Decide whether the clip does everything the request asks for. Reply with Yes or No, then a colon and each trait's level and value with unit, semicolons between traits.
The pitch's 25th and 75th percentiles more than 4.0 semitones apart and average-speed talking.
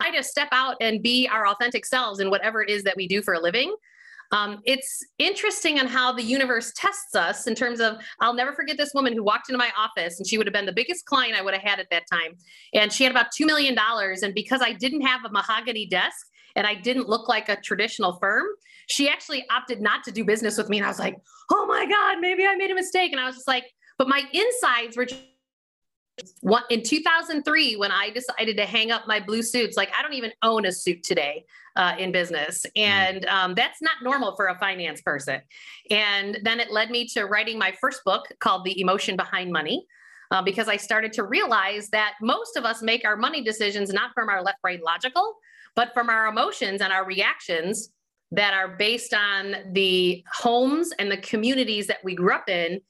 No: average, 4.6 semitones; fast, 225 wpm